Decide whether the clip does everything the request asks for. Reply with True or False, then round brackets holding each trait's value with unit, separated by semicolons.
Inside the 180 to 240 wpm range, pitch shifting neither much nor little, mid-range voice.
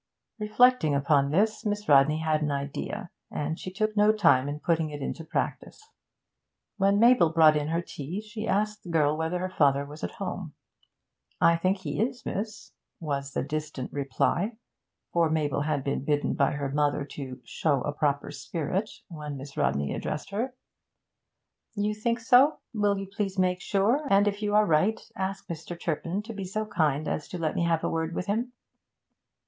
False (185 wpm; 5.8 semitones; 170 Hz)